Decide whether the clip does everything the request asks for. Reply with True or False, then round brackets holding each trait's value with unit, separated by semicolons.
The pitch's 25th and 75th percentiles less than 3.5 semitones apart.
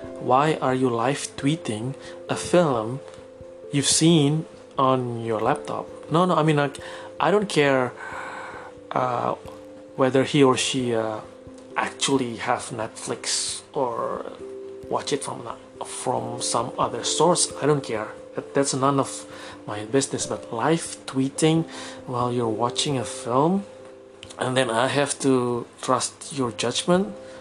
False (4.2 semitones)